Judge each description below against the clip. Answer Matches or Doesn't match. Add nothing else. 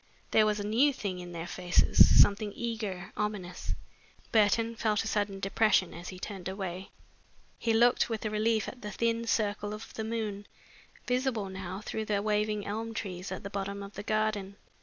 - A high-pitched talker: Matches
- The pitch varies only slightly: Matches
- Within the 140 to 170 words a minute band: Doesn't match